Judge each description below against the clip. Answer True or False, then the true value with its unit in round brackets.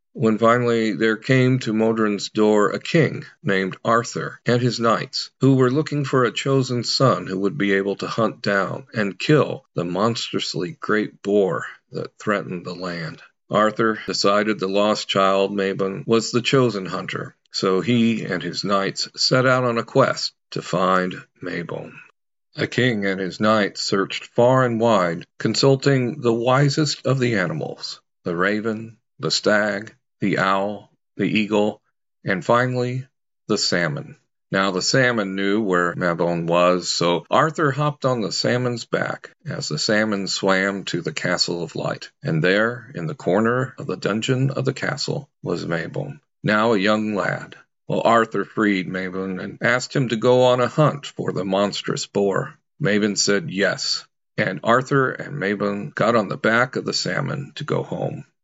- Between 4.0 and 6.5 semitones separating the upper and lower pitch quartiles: True (4.3 semitones)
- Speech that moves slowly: False (165 wpm)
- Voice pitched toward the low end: True (110 Hz)